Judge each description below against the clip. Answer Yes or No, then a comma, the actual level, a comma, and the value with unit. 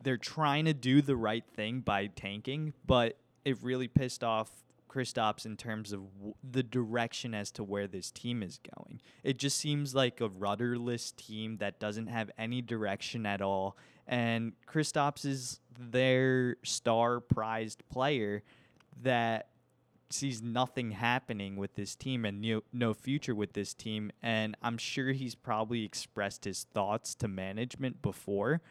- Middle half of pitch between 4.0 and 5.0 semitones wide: No, average, 3.2 semitones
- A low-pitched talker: Yes, low, 120 Hz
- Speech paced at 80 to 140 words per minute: No, average, 155 wpm